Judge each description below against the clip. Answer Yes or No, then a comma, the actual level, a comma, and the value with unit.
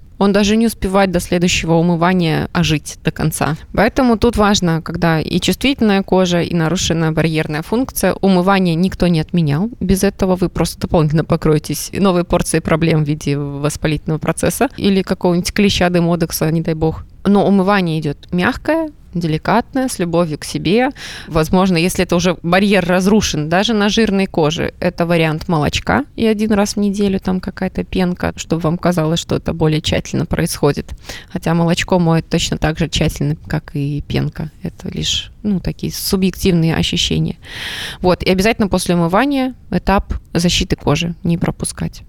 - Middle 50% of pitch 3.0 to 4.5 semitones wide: Yes, average, 3.5 semitones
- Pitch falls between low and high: Yes, medium, 175 Hz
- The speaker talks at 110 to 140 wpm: No, average, 155 wpm